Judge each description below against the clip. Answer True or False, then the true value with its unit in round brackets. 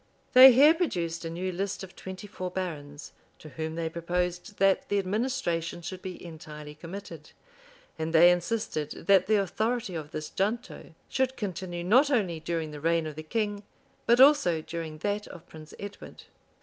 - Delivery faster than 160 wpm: True (170 wpm)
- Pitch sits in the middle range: True (180 Hz)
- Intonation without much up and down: False (4.0 semitones)